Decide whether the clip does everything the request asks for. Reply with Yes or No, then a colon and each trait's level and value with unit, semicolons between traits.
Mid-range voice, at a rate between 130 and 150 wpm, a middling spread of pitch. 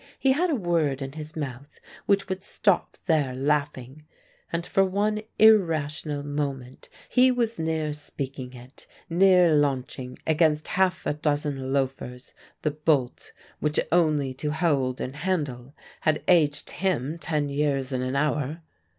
Yes: medium, 150 Hz; average, 140 wpm; average, 4.0 semitones